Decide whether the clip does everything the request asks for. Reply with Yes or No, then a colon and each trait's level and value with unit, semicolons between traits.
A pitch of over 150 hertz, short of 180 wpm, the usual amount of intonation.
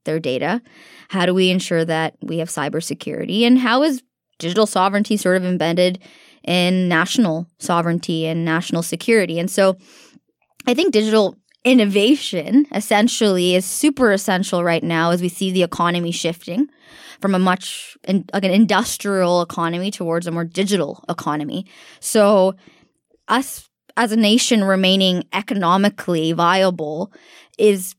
Yes: medium, 185 Hz; slow, 135 wpm; average, 3.9 semitones